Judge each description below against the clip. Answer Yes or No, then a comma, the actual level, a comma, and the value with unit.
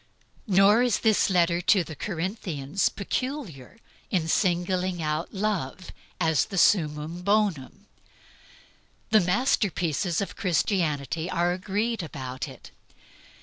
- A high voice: No, medium, 180 Hz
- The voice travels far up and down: No, average, 4.0 semitones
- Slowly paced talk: Yes, slow, 105 wpm